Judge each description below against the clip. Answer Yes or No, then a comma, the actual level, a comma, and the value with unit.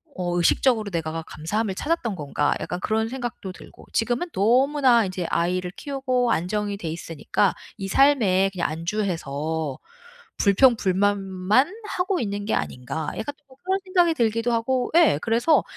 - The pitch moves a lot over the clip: Yes, wide, 6.2 semitones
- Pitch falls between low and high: No, high, 210 Hz